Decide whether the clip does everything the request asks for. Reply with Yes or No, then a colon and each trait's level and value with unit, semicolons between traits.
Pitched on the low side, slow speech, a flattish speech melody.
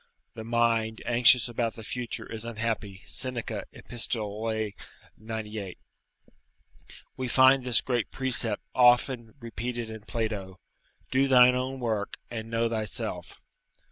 Yes: low, 115 Hz; slow, 115 wpm; narrow, 2.0 semitones